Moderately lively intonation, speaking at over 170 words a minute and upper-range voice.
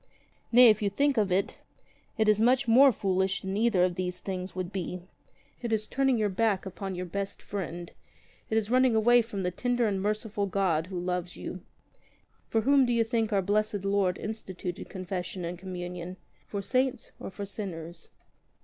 Yes: average, 3.5 semitones; average, 185 wpm; high, 200 Hz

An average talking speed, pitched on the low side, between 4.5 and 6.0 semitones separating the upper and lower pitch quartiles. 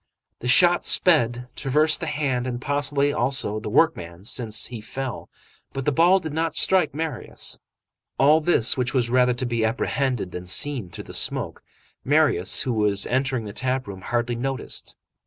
No: average, 170 wpm; low, 130 Hz; average, 3.8 semitones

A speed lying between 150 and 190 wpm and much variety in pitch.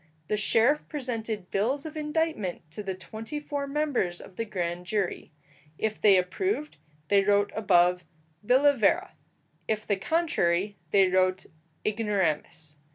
No: slow, 135 wpm; wide, 7.1 semitones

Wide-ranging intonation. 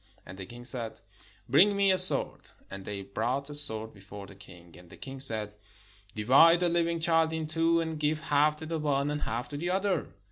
Yes: wide, 6.9 semitones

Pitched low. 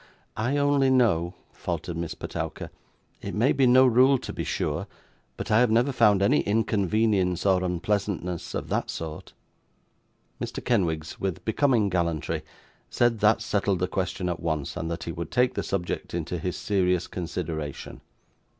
Yes: very low, 95 Hz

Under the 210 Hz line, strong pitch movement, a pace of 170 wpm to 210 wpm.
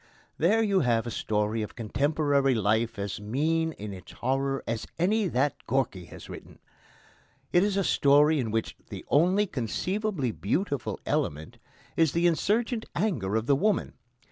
No: medium, 140 Hz; wide, 7.8 semitones; average, 155 wpm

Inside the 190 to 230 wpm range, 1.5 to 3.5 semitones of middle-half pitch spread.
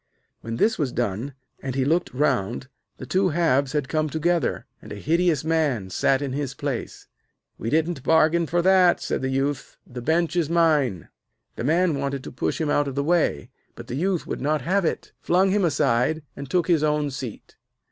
No: average, 200 wpm; average, 4.3 semitones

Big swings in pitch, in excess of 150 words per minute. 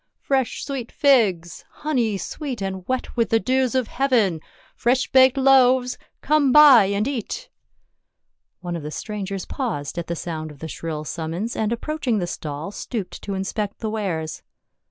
Yes: wide, 6.7 semitones; average, 170 wpm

